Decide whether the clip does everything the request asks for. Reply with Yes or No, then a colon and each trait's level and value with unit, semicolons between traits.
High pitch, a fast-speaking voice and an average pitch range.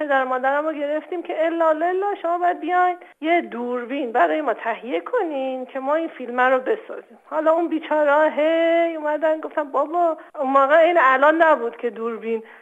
Yes: very high, 310 Hz; fast, 170 wpm; average, 4.0 semitones